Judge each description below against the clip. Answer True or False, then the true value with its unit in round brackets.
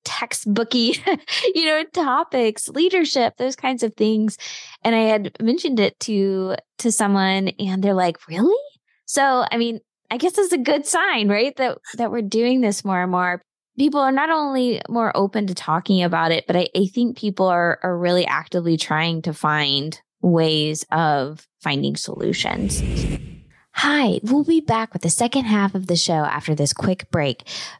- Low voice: False (215 Hz)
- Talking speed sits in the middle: True (175 wpm)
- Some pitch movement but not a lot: False (6.3 semitones)